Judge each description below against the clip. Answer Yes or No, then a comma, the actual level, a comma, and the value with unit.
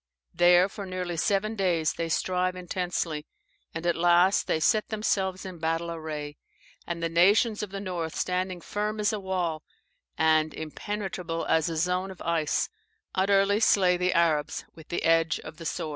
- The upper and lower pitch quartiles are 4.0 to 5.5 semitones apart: No, narrow, 2.6 semitones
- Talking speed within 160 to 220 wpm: Yes, average, 170 wpm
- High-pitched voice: No, medium, 175 Hz